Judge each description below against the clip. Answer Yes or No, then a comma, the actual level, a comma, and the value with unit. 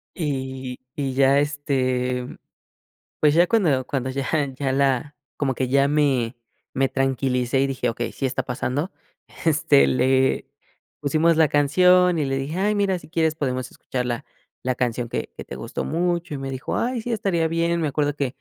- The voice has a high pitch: No, medium, 140 Hz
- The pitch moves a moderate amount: Yes, average, 3.7 semitones